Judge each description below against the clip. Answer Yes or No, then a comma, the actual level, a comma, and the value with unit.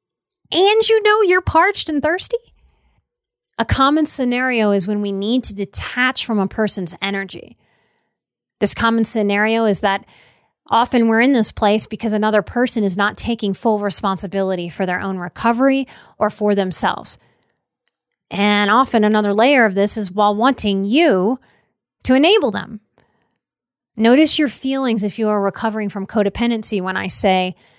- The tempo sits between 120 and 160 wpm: Yes, average, 150 wpm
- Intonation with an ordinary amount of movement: Yes, average, 4.1 semitones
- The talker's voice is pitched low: No, high, 215 Hz